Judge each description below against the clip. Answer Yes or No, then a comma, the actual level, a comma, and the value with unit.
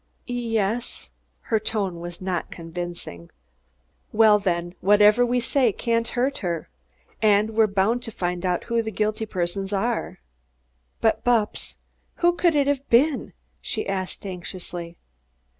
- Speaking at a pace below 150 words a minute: Yes, average, 140 wpm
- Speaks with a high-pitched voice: Yes, high, 210 Hz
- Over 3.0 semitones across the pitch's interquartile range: Yes, average, 4.4 semitones